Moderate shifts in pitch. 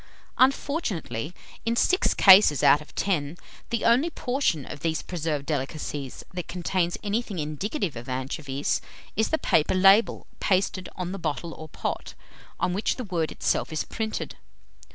No: wide, 6.1 semitones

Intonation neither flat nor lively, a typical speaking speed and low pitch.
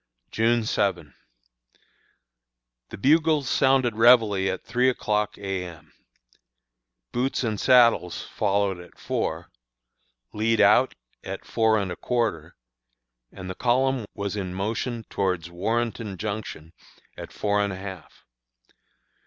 No: average, 3.8 semitones; slow, 120 wpm; low, 105 Hz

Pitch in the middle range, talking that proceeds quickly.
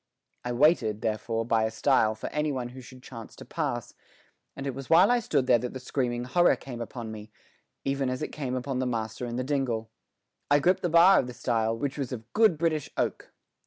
No: low, 125 Hz; fast, 225 wpm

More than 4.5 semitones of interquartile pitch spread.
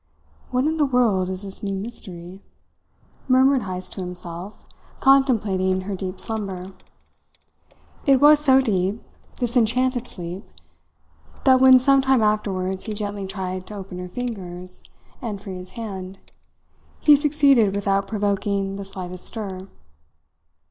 Yes: average, 4.9 semitones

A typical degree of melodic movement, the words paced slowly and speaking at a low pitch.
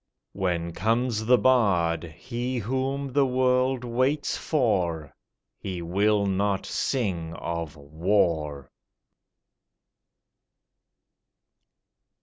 No: wide, 7.0 semitones; slow, 80 wpm; low, 105 Hz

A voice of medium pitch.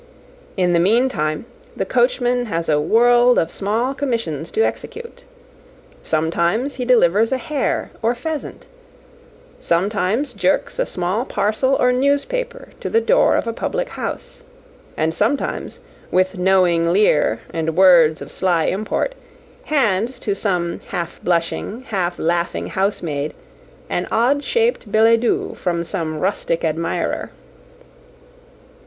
No: high, 205 Hz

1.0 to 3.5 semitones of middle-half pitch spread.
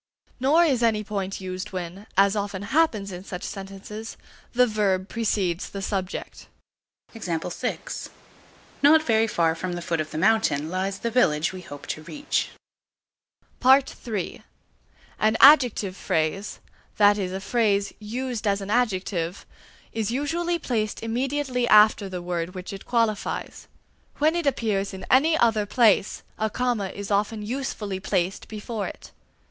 No: average, 4.0 semitones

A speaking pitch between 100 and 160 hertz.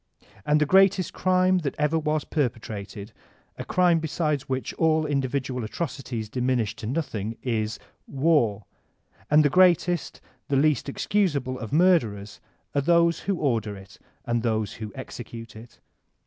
Yes: medium, 140 Hz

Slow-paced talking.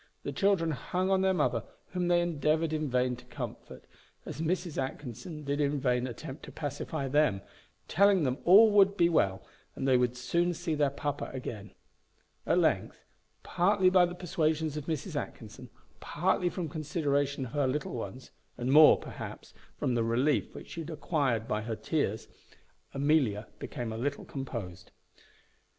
No: average, 165 wpm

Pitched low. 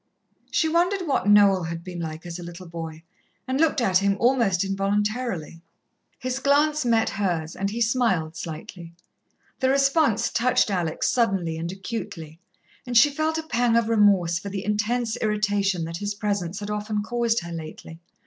No: high, 205 Hz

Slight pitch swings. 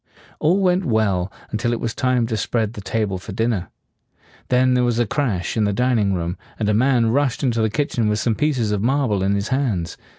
No: average, 3.6 semitones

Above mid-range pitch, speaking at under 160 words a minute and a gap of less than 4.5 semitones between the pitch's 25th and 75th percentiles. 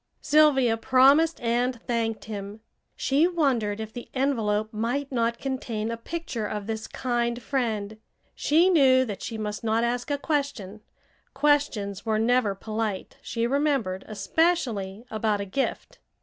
Yes: high, 235 Hz; average, 140 wpm; average, 4.1 semitones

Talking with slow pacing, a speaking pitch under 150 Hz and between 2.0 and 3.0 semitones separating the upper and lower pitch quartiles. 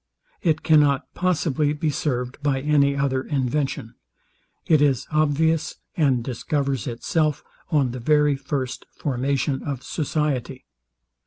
Yes: slow, 115 wpm; medium, 140 Hz; narrow, 2.4 semitones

